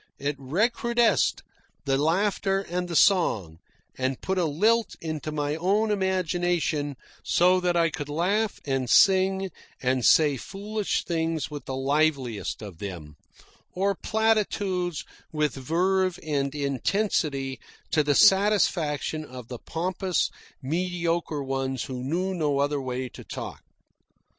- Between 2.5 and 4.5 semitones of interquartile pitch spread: No, average, 5.3 semitones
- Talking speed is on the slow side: Yes, slow, 130 wpm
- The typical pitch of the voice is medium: Yes, medium, 160 Hz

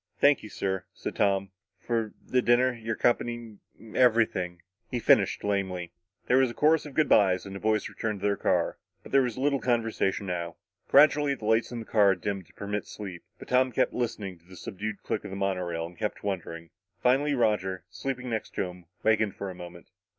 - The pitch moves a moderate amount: Yes, average, 4.2 semitones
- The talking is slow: No, fast, 205 wpm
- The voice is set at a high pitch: No, low, 105 Hz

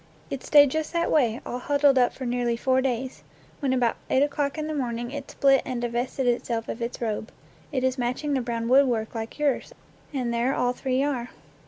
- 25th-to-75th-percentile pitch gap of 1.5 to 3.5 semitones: Yes, average, 2.8 semitones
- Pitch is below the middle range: No, very high, 255 Hz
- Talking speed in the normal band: No, fast, 210 wpm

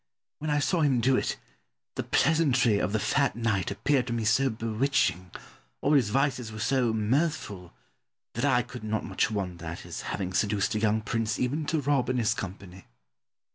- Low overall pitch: Yes, low, 115 Hz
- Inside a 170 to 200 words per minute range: Yes, average, 185 wpm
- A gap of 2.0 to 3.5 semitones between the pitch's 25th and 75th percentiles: No, average, 4.5 semitones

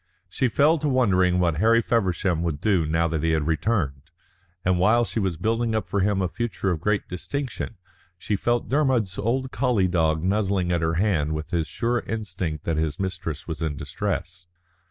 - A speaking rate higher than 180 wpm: Yes, average, 190 wpm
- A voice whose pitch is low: Yes, very low, 95 Hz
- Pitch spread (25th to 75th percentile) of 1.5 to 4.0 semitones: No, wide, 5.6 semitones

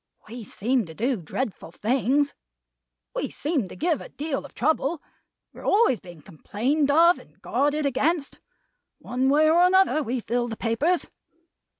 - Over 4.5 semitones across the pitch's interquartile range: Yes, average, 5.0 semitones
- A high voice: Yes, very high, 275 Hz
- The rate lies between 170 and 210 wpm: No, average, 160 wpm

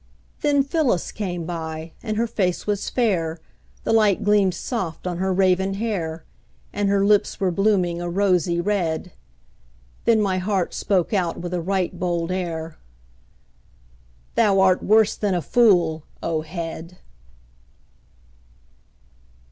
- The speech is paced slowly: Yes, slow, 130 wpm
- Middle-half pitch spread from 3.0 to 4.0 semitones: Yes, average, 3.3 semitones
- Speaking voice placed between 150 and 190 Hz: Yes, medium, 185 Hz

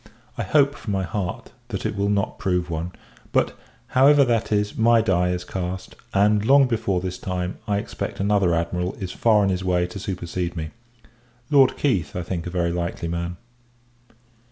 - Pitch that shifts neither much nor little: Yes, average, 3.0 semitones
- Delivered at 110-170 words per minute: No, average, 180 wpm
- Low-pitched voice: Yes, very low, 95 Hz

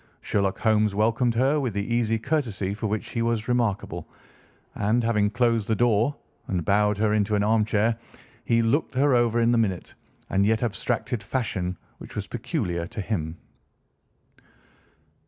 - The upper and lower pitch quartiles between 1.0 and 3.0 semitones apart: Yes, narrow, 2.5 semitones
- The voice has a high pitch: No, low, 110 Hz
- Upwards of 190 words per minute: No, average, 155 wpm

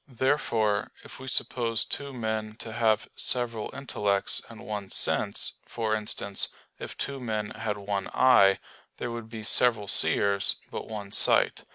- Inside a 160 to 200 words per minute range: No, average, 150 wpm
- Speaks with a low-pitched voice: Yes, low, 110 Hz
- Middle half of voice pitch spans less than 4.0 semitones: Yes, narrow, 2.6 semitones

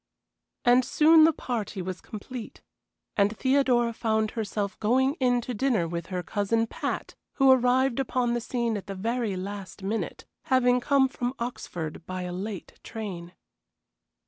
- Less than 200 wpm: Yes, average, 150 wpm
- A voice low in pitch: No, high, 230 Hz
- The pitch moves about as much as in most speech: Yes, average, 4.0 semitones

